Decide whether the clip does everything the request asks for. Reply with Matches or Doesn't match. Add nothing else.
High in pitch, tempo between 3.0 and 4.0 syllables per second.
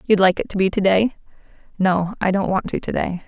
Doesn't match